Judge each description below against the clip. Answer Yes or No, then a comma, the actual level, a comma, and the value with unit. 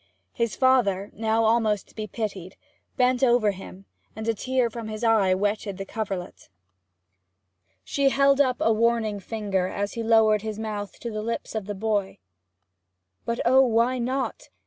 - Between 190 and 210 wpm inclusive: No, average, 165 wpm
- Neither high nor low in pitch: No, high, 220 Hz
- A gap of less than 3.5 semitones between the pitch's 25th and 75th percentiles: Yes, narrow, 2.5 semitones